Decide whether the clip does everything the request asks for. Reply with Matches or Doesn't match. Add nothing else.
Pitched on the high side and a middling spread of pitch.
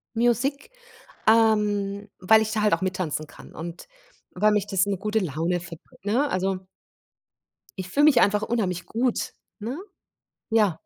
Matches